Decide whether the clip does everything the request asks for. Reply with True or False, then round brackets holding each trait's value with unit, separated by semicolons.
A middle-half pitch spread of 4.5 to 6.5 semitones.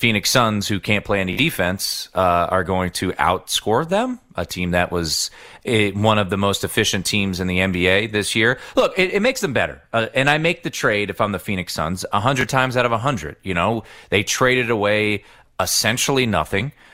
True (4.9 semitones)